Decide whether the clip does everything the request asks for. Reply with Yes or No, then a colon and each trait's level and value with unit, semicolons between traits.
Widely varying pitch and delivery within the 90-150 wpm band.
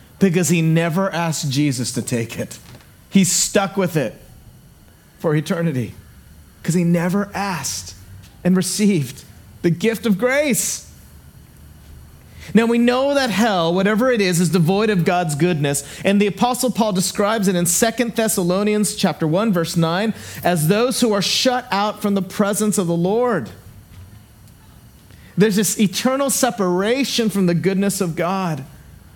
Yes: wide, 6.6 semitones; average, 145 wpm